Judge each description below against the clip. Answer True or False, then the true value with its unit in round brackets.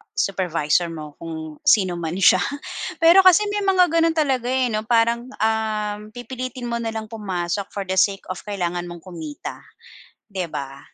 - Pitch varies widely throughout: True (5.9 semitones)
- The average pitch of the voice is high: True (205 Hz)